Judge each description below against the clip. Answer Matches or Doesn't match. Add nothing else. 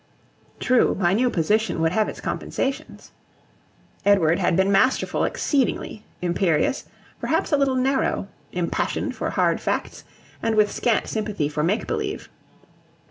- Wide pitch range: Matches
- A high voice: Matches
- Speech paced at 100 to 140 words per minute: Matches